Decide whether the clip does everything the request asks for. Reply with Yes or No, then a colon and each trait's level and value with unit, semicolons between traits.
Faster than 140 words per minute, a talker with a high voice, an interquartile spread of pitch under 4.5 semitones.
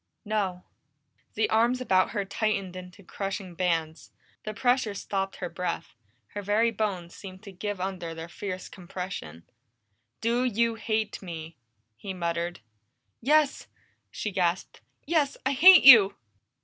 No: slow, 135 wpm; high, 195 Hz; average, 3.7 semitones